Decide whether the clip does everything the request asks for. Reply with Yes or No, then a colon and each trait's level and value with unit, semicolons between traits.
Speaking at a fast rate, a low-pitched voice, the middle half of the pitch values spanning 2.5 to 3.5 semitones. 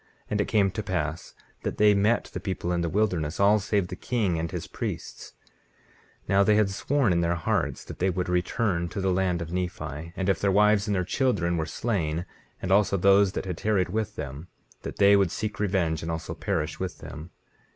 Yes: fast, 215 wpm; very low, 95 Hz; average, 3.1 semitones